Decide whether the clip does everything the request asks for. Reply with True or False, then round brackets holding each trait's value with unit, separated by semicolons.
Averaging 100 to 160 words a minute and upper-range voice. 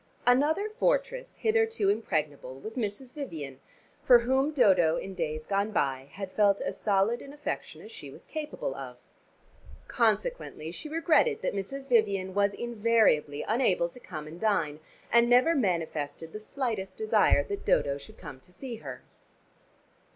True (150 wpm; 215 Hz)